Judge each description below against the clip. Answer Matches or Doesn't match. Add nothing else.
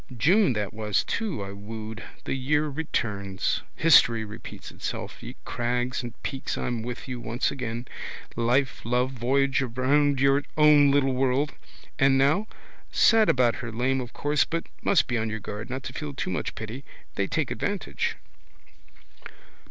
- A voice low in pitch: Matches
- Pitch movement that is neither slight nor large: Matches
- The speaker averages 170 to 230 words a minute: Doesn't match